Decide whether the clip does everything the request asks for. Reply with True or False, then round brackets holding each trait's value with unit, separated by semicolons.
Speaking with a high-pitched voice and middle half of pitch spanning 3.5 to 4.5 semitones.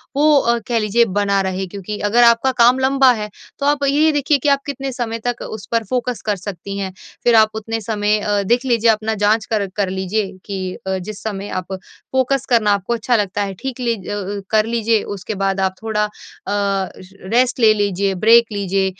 False (215 Hz; 3.1 semitones)